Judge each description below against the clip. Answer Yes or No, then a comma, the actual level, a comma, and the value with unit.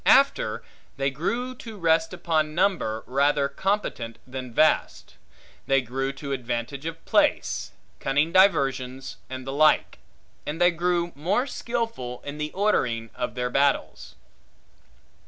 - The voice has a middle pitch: Yes, medium, 145 Hz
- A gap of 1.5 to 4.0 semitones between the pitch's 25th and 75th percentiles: No, average, 5.1 semitones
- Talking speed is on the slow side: Yes, slow, 130 wpm